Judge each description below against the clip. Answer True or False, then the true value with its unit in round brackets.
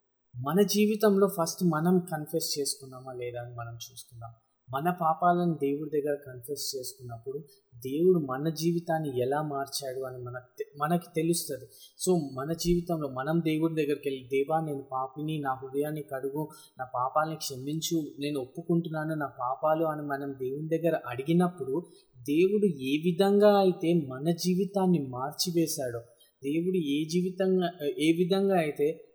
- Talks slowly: True (130 wpm)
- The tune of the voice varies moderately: True (4.3 semitones)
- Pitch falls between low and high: True (155 Hz)